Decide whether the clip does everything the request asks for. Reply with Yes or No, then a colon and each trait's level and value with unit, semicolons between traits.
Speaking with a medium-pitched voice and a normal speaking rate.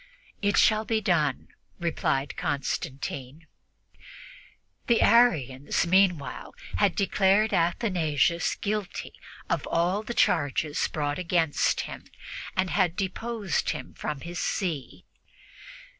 No: medium, 175 Hz; slow, 100 wpm